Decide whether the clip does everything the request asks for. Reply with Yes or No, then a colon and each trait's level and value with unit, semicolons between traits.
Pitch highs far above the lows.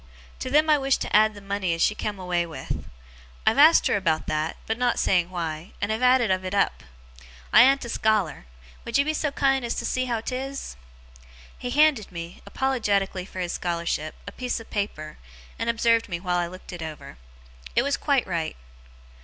Yes: wide, 6.3 semitones